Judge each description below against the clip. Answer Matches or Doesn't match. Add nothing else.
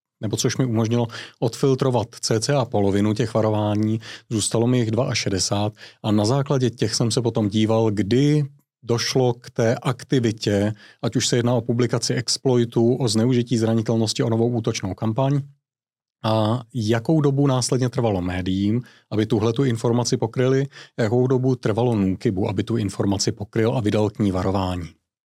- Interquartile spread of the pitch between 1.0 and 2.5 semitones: Doesn't match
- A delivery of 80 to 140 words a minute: Doesn't match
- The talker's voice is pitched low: Matches